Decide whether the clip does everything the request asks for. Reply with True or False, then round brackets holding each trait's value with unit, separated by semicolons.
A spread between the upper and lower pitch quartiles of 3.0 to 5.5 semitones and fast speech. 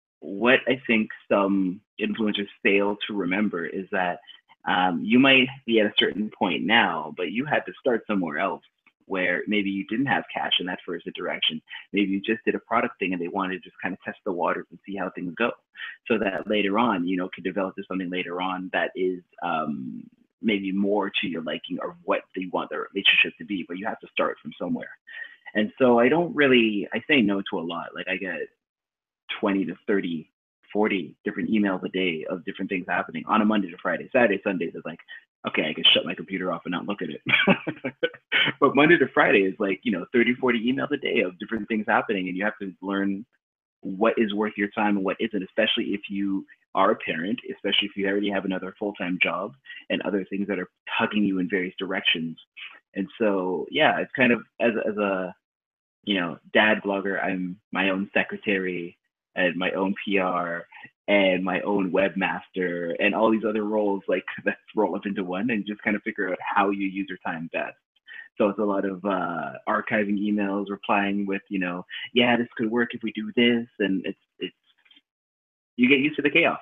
False (2.5 semitones; 210 wpm)